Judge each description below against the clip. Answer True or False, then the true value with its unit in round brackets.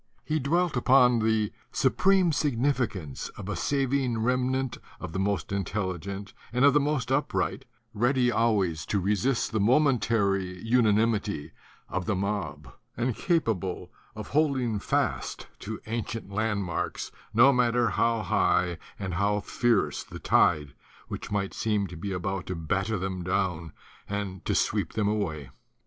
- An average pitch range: True (4.5 semitones)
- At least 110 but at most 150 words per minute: True (140 wpm)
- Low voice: True (105 Hz)